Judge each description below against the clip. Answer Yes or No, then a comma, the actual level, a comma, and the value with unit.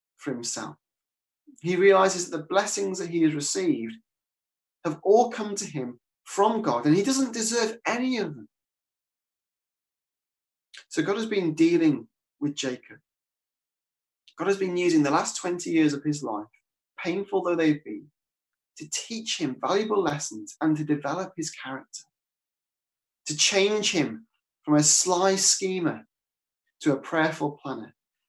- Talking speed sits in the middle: Yes, average, 145 wpm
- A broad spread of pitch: Yes, wide, 5.8 semitones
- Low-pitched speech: No, medium, 180 Hz